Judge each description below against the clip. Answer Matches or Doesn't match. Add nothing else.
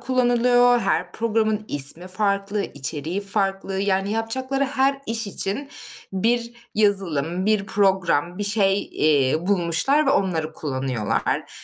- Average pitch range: Matches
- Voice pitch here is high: Matches